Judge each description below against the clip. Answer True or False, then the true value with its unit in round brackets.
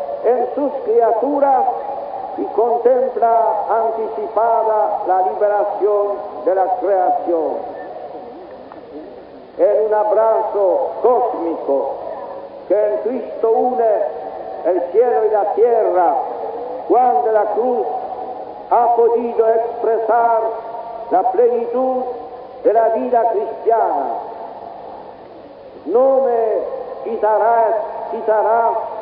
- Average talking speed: False (85 wpm)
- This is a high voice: True (230 Hz)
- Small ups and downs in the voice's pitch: True (2.3 semitones)